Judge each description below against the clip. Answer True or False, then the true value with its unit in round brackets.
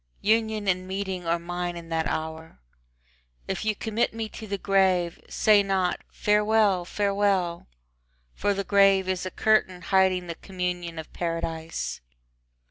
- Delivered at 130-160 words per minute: True (140 wpm)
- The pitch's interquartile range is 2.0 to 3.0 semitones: True (2.7 semitones)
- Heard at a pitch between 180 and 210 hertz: True (185 Hz)